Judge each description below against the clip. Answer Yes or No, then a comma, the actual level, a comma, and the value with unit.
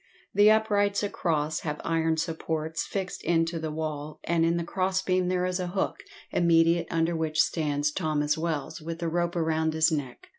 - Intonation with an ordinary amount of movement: No, narrow, 2.2 semitones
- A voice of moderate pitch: Yes, medium, 165 Hz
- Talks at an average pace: Yes, average, 175 wpm